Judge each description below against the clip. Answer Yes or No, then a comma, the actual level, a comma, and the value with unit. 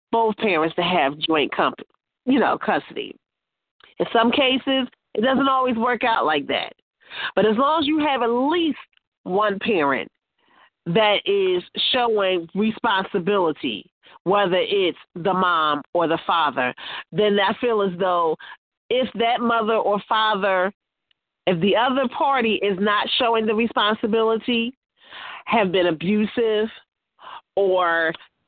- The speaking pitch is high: Yes, high, 220 Hz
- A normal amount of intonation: Yes, average, 4.5 semitones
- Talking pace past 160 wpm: No, slow, 135 wpm